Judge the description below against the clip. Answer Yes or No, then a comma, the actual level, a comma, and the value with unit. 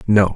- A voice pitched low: Yes, low, 100 Hz